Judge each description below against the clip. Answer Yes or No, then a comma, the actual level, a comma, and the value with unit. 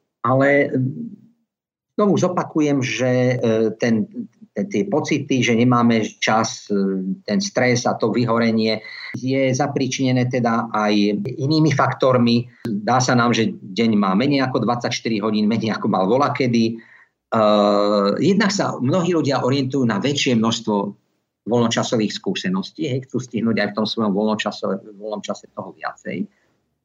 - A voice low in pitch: Yes, low, 125 Hz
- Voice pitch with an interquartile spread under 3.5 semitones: No, average, 4.1 semitones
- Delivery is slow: No, average, 125 wpm